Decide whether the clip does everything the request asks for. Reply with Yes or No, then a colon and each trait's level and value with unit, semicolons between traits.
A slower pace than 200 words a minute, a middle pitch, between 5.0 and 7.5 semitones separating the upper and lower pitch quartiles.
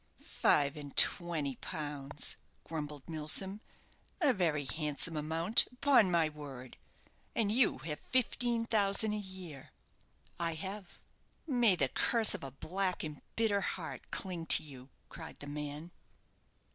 Yes: slow, 135 wpm; medium, 165 Hz; average, 5.3 semitones